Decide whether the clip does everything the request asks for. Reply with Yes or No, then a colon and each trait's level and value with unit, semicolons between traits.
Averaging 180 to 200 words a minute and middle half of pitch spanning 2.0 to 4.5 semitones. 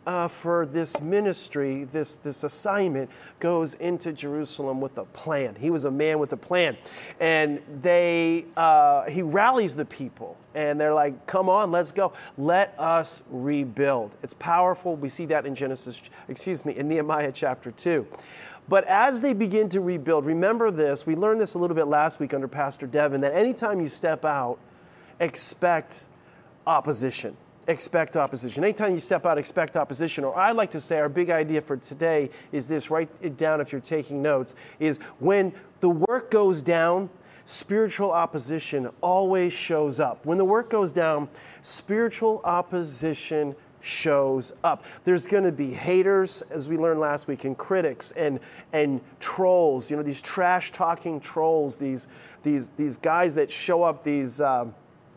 No: average, 165 wpm; average, 3.8 semitones